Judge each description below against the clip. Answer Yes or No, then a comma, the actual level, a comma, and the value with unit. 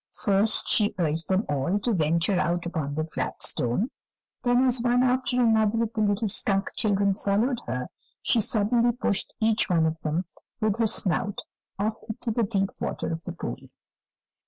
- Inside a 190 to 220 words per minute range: No, average, 175 wpm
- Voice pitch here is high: Yes, high, 205 Hz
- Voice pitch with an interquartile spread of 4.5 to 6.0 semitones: Yes, average, 5.0 semitones